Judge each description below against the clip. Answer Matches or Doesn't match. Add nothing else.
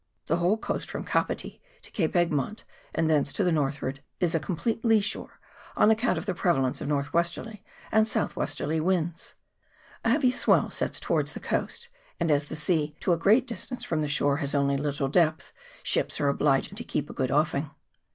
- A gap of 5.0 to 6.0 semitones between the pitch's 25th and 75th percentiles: Matches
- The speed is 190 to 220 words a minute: Matches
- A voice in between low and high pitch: Matches